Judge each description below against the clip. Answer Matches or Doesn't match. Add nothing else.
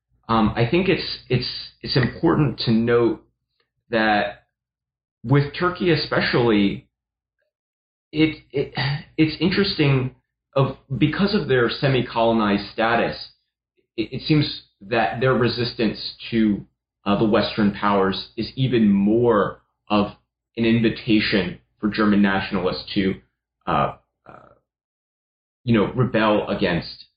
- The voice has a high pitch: Doesn't match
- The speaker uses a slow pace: Matches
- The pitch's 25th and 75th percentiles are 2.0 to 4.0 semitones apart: Doesn't match